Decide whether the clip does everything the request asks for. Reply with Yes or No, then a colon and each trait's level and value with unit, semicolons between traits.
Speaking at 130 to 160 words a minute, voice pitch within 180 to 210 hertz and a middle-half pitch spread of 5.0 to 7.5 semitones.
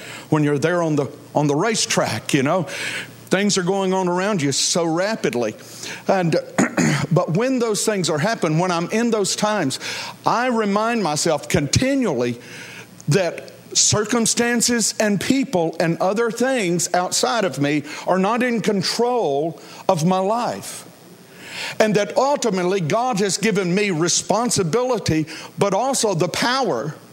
Yes: average, 140 wpm; high, 190 Hz; wide, 5.4 semitones